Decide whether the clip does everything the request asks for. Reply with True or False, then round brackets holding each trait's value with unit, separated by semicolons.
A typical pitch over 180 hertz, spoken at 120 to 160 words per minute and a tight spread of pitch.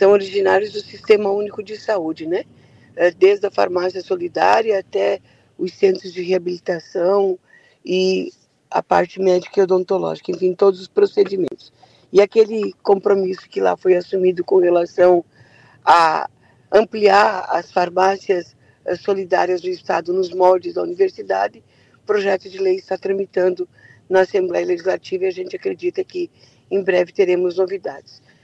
True (190 Hz; 135 wpm; 2.1 semitones)